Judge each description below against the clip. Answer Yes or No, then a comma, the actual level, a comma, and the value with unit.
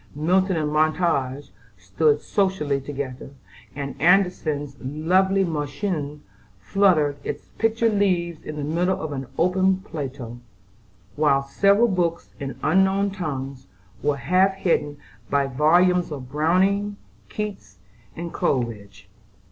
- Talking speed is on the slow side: Yes, slow, 115 wpm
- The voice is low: No, medium, 155 Hz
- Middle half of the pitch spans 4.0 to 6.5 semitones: Yes, average, 5.2 semitones